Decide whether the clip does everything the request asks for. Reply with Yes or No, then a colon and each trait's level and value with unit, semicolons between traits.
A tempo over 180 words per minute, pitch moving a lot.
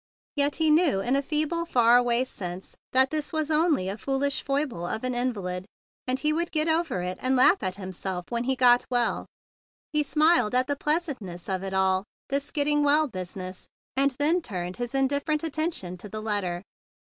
Yes: average, 190 wpm; wide, 7.6 semitones